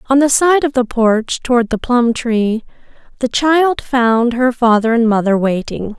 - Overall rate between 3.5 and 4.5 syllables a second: Yes, 4.2 syllables/s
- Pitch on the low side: No, high, 240 Hz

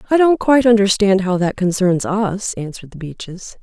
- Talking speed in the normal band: Yes, average, 180 wpm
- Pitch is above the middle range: Yes, high, 200 Hz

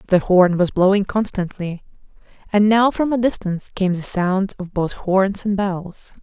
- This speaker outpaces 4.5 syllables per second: No, 4.4 syllables/s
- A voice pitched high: Yes, high, 195 Hz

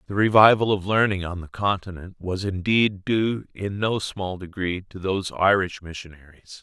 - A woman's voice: No, male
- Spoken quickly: No, average, 165 wpm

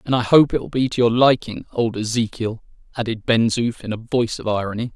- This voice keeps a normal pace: No, fast, 230 wpm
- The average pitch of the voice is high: No, low, 115 Hz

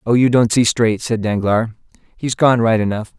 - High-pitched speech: No, low, 115 Hz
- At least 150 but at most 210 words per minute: Yes, fast, 205 wpm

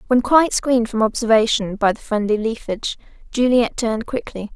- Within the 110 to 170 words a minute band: Yes, average, 160 wpm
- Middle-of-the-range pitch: No, high, 225 Hz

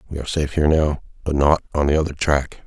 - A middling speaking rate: No, fast, 250 wpm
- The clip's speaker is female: No, male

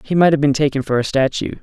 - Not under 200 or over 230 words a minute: No, fast, 295 wpm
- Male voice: Yes, male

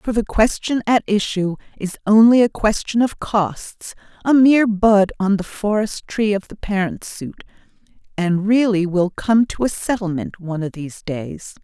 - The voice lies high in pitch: Yes, high, 205 Hz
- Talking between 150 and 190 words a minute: Yes, average, 170 wpm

